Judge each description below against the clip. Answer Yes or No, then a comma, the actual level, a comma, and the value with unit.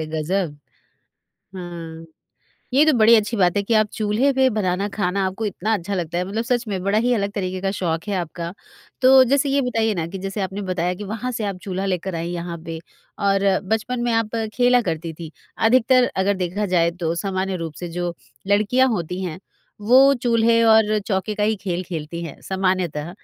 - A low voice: No, high, 195 Hz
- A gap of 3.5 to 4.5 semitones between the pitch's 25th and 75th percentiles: Yes, average, 4.0 semitones